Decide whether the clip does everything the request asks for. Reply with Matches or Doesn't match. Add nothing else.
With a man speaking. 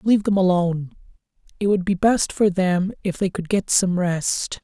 Matches